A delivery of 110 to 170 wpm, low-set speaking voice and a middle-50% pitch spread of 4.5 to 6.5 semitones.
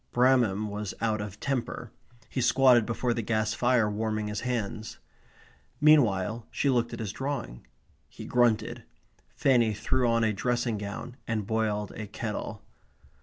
No: average, 145 wpm; low, 115 Hz; narrow, 2.6 semitones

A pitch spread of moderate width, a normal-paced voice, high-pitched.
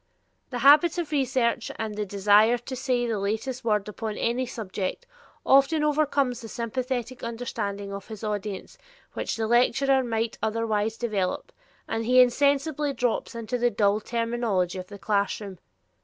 Yes: average, 3.3 semitones; average, 150 wpm; high, 230 Hz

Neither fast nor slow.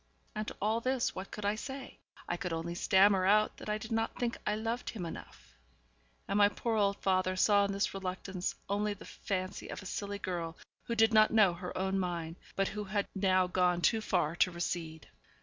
No: fast, 210 wpm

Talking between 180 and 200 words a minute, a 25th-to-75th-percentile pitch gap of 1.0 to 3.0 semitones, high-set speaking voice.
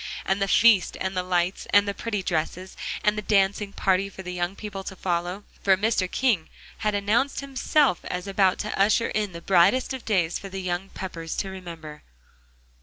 Yes: average, 190 wpm; narrow, 2.6 semitones; high, 195 Hz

